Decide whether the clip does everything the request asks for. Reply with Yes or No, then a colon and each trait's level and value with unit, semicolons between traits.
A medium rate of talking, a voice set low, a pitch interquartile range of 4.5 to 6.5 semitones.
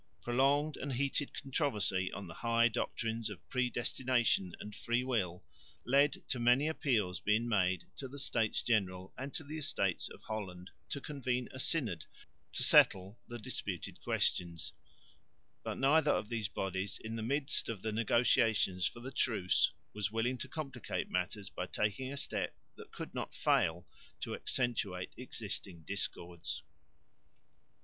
Yes: average, 145 wpm; low, 115 Hz; average, 5.2 semitones